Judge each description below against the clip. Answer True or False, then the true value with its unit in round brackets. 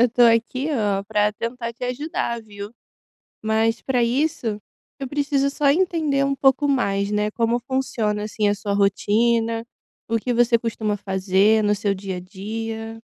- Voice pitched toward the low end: False (225 Hz)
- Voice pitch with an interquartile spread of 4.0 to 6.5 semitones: False (3.4 semitones)